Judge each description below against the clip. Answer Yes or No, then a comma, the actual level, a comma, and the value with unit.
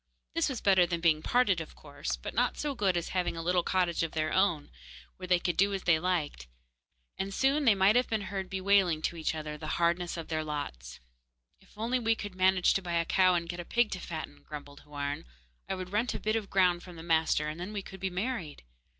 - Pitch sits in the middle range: Yes, medium, 180 Hz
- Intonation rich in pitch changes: No, average, 3.6 semitones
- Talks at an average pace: No, fast, 240 wpm